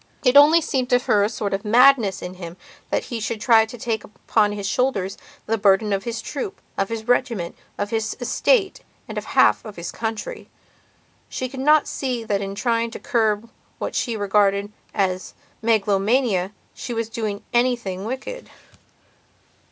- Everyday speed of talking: Yes, average, 175 wpm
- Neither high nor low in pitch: No, high, 220 Hz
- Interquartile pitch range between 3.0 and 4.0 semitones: Yes, average, 3.4 semitones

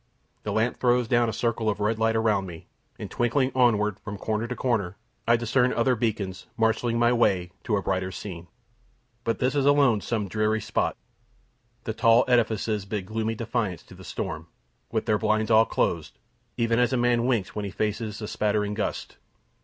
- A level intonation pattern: Yes, narrow, 2.3 semitones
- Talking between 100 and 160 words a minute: No, average, 190 wpm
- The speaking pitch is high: No, low, 110 Hz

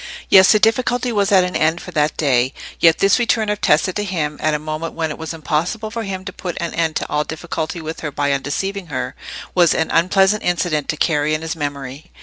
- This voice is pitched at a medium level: Yes, medium, 165 Hz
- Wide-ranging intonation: No, average, 4.1 semitones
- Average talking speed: No, fast, 230 wpm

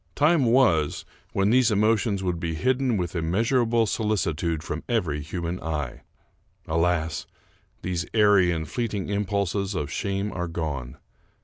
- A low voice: Yes, very low, 95 Hz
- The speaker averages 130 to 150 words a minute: Yes, slow, 135 wpm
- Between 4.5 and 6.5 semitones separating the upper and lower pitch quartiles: Yes, average, 5.0 semitones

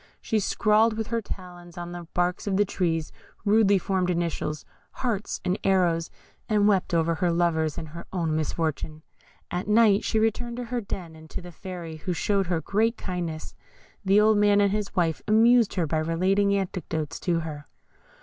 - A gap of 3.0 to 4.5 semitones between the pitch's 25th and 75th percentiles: Yes, average, 3.8 semitones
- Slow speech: No, average, 180 wpm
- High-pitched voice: No, medium, 180 Hz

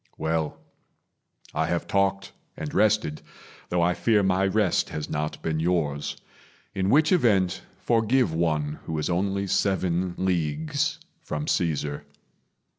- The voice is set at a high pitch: No, very low, 90 Hz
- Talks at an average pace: No, slow, 125 wpm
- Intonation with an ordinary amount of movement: Yes, average, 4.0 semitones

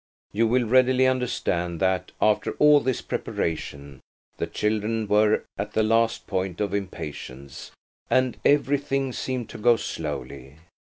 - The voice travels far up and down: Yes, wide, 6.3 semitones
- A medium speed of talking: No, slow, 130 wpm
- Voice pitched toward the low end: Yes, low, 110 Hz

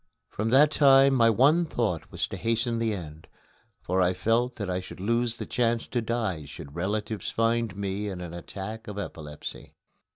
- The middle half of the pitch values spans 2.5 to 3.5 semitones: No, average, 4.2 semitones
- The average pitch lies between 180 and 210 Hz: No, low, 110 Hz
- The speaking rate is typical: Yes, average, 185 wpm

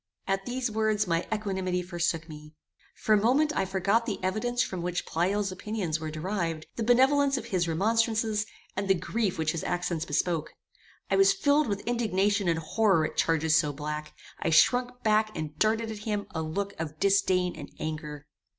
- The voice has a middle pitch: No, high, 195 Hz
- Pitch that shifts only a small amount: No, average, 5.0 semitones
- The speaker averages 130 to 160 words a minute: No, average, 180 wpm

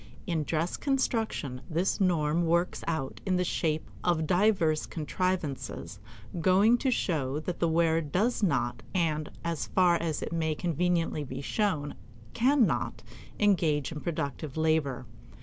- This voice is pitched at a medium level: Yes, medium, 165 Hz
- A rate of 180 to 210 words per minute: No, average, 140 wpm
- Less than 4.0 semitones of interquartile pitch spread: Yes, average, 3.4 semitones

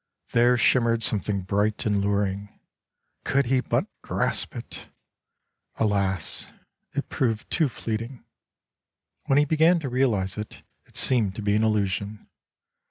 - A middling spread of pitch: Yes, average, 3.8 semitones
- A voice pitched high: No, low, 110 Hz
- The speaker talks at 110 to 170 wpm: Yes, slow, 135 wpm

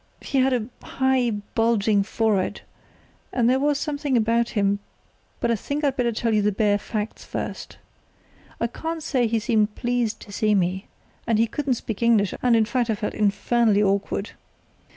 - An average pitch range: Yes, average, 3.0 semitones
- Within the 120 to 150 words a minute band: No, average, 170 wpm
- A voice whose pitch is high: Yes, high, 230 Hz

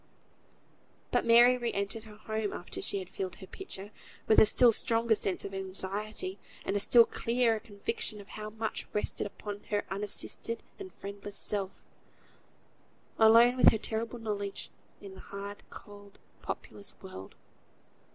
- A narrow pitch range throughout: Yes, narrow, 2.3 semitones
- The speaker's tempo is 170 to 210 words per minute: No, average, 150 wpm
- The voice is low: No, high, 210 Hz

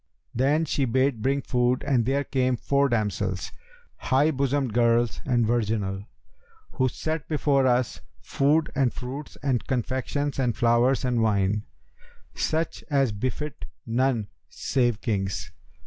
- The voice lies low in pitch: Yes, low, 125 Hz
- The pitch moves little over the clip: No, average, 3.2 semitones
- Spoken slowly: Yes, slow, 130 wpm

